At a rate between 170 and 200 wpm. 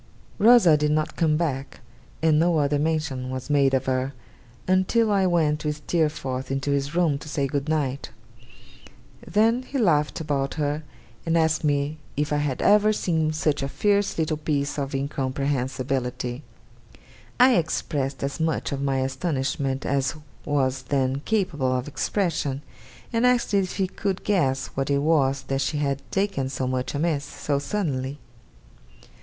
No: average, 155 wpm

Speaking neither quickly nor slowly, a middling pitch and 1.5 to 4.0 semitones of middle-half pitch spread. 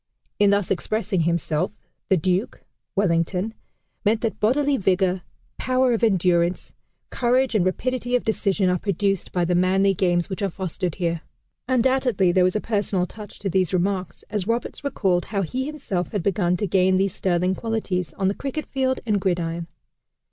No: average, 170 wpm; high, 195 Hz; average, 3.7 semitones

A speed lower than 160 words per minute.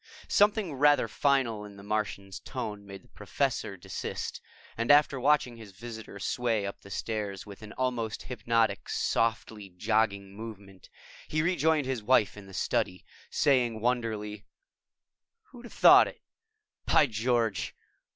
Yes: average, 140 wpm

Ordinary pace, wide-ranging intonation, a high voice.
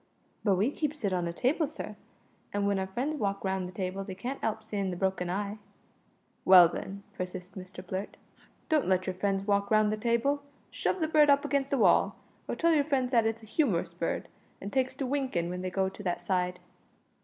No: fast, 215 wpm; wide, 5.7 semitones; high, 200 Hz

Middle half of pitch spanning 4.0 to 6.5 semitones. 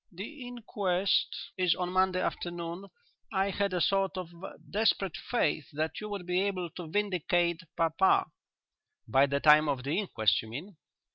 No: average, 3.5 semitones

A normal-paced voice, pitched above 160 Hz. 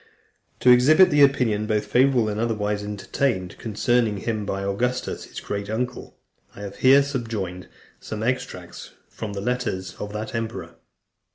No: average, 150 wpm; low, 110 Hz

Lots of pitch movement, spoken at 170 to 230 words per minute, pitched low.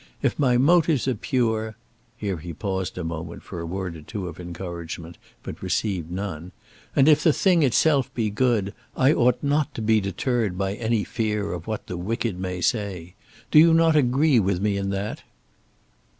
Yes: wide, 5.8 semitones; average, 185 wpm; low, 105 Hz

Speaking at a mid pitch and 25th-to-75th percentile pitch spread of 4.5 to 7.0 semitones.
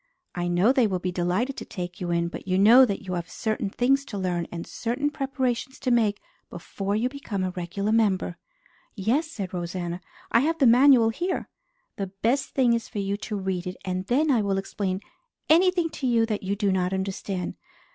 No: high, 205 Hz; average, 5.2 semitones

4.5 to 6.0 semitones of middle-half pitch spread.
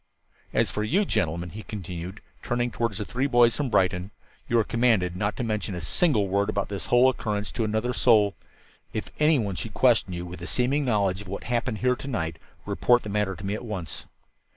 No: average, 4.1 semitones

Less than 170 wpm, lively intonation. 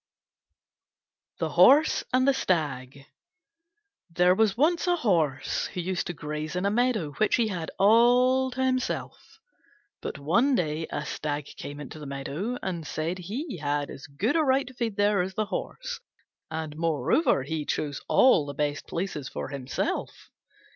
Yes: average, 160 wpm; wide, 8.6 semitones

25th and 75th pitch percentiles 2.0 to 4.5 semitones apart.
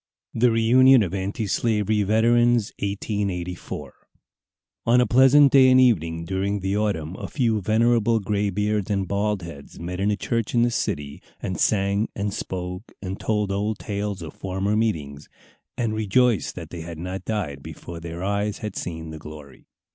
Yes: average, 3.7 semitones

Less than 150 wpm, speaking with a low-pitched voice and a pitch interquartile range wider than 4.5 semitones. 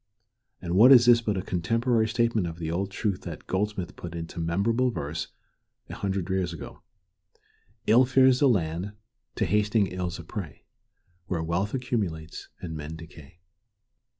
No: average, 155 wpm; very low, 95 Hz; average, 5.3 semitones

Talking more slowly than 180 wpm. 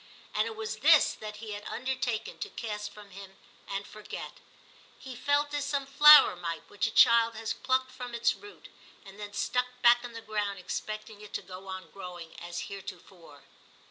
No: average, 185 wpm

